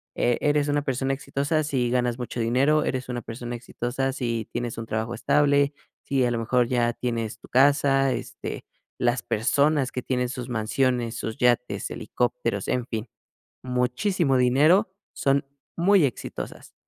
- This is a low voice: Yes, low, 125 Hz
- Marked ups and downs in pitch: No, average, 2.8 semitones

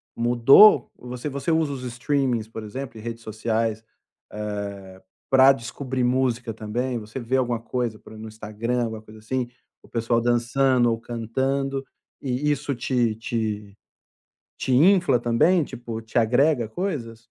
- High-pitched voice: No, low, 120 Hz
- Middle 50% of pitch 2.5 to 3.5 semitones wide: Yes, average, 2.9 semitones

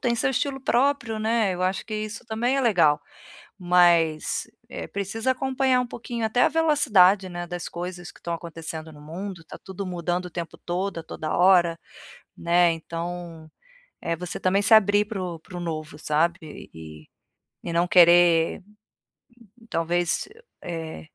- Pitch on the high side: No, medium, 180 Hz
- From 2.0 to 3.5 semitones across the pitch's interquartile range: No, average, 4.4 semitones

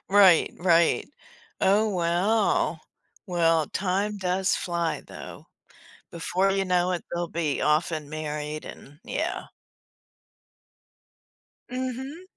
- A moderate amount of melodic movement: Yes, average, 3.1 semitones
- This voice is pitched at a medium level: Yes, medium, 175 Hz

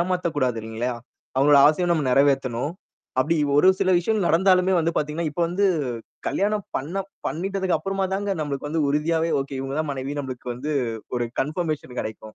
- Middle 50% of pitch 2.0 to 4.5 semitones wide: No, average, 5.0 semitones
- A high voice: No, medium, 155 Hz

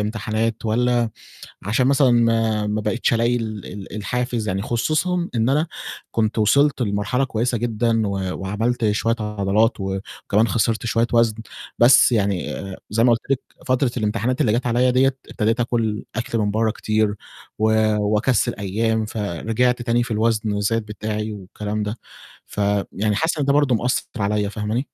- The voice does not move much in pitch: Yes, narrow, 2.3 semitones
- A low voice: Yes, low, 110 Hz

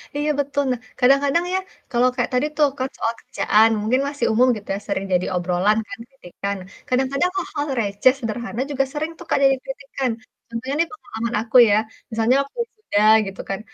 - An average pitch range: Yes, average, 4.2 semitones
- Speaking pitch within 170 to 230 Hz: No, very high, 255 Hz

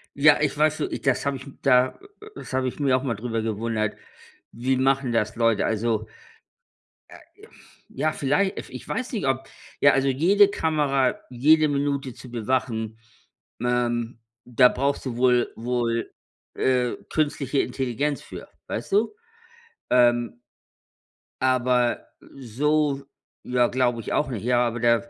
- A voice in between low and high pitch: No, low, 130 Hz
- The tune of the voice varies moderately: Yes, average, 3.0 semitones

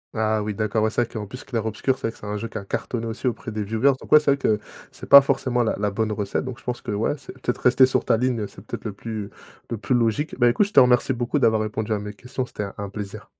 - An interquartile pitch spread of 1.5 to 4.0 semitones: Yes, average, 2.9 semitones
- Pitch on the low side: Yes, low, 115 Hz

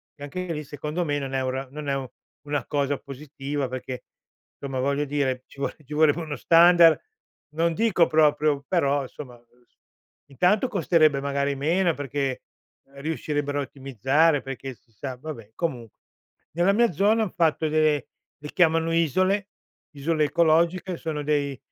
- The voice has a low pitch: No, medium, 145 Hz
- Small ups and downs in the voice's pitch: No, average, 3.1 semitones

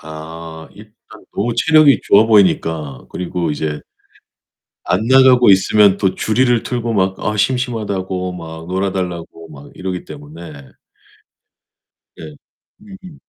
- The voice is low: Yes, very low, 95 Hz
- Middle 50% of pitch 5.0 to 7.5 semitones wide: Yes, wide, 5.6 semitones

